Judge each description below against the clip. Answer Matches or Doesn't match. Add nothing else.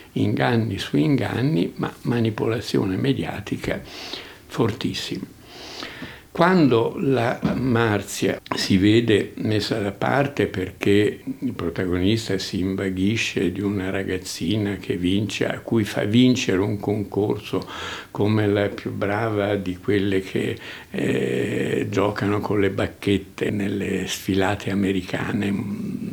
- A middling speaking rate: Doesn't match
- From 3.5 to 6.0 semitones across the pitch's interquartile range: Doesn't match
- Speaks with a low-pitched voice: Matches